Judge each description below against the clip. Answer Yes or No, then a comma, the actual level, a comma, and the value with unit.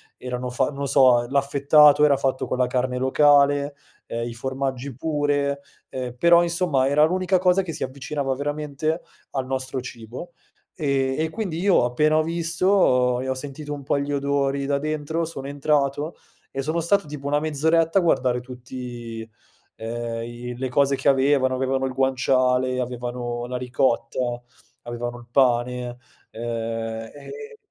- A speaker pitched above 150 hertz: No, low, 135 Hz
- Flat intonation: No, average, 3.0 semitones